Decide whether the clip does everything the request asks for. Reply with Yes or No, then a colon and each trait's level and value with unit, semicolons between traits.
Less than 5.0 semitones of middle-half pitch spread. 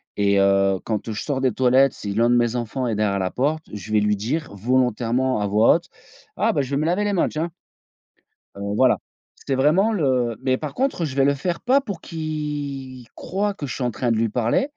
No: wide, 5.6 semitones